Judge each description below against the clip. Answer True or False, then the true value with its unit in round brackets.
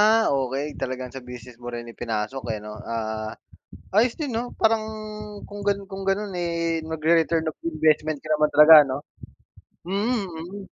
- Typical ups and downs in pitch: False (8.0 semitones)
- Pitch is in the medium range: True (155 Hz)